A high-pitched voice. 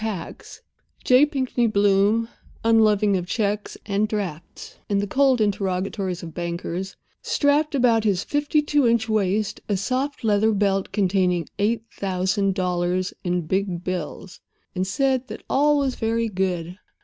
Yes: high, 205 Hz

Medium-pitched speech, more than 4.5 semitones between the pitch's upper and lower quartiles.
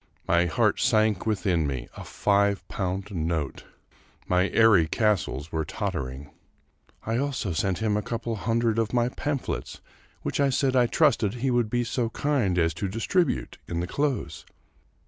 No: low, 105 Hz; average, 5.3 semitones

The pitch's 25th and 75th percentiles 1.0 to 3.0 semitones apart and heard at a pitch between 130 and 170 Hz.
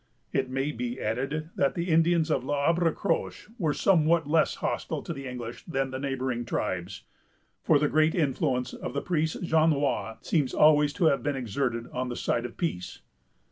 No: average, 4.0 semitones; medium, 140 Hz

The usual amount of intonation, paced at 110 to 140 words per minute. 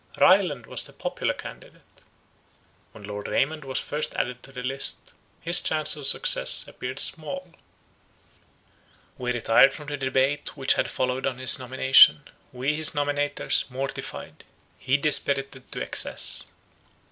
No: narrow, 2.3 semitones; slow, 135 wpm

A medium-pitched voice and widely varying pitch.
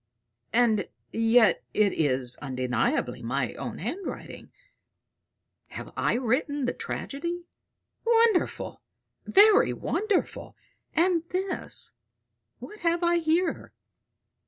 No: very high, 315 Hz; wide, 8.3 semitones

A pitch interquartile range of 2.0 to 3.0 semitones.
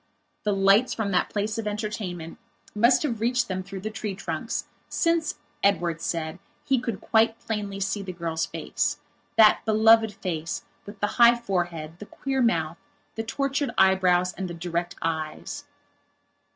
No: average, 4.2 semitones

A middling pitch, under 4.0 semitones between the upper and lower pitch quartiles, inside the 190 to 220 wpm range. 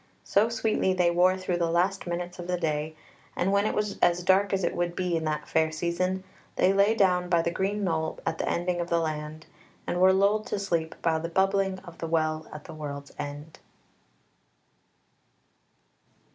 Yes: medium, 175 Hz; average, 2.8 semitones; average, 195 wpm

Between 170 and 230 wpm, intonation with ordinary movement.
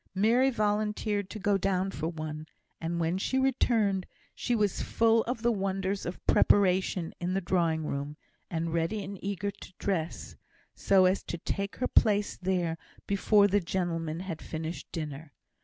No: average, 160 wpm; average, 3.6 semitones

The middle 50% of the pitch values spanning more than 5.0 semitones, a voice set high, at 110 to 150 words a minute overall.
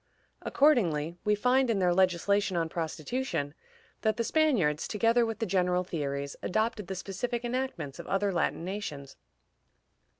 Yes: wide, 5.6 semitones; high, 195 Hz; average, 140 wpm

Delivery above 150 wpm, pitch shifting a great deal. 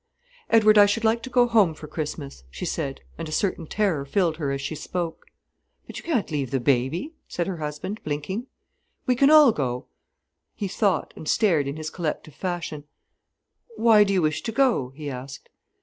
Yes: average, 185 wpm; wide, 6.5 semitones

